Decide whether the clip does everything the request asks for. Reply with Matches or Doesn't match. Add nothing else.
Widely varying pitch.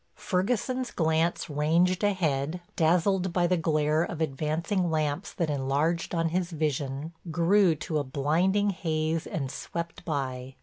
Doesn't match